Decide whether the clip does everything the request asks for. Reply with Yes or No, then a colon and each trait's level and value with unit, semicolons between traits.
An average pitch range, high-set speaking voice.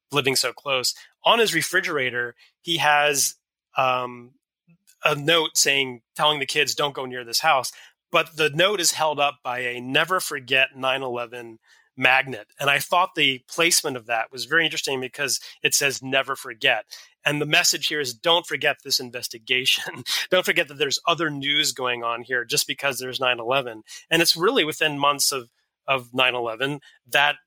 No: average, 3.3 semitones; medium, 140 Hz